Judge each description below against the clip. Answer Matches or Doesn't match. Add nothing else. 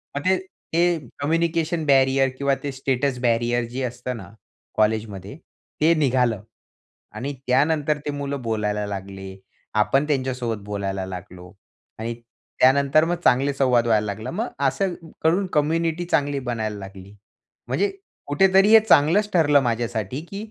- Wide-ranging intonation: Matches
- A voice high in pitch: Doesn't match